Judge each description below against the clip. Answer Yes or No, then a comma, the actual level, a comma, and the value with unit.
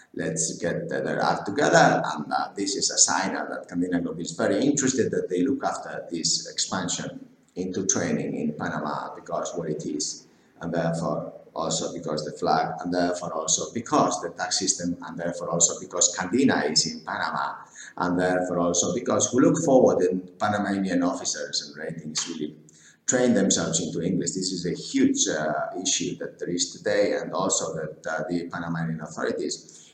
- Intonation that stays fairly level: Yes, narrow, 2.1 semitones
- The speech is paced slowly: No, average, 175 wpm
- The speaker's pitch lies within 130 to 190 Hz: No, very low, 90 Hz